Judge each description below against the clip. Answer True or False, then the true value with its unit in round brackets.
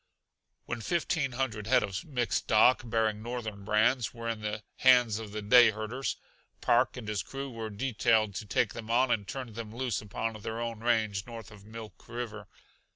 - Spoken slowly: False (185 wpm)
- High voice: False (115 Hz)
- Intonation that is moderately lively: False (2.3 semitones)